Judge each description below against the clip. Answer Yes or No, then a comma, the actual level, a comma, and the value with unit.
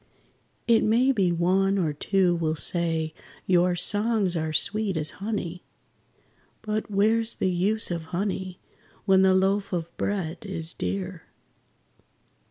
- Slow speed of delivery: Yes, slow, 130 wpm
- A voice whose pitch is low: No, medium, 185 Hz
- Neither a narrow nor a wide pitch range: Yes, average, 3.3 semitones